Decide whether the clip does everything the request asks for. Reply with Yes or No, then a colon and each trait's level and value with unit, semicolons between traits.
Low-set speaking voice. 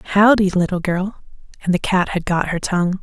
No: medium, 185 Hz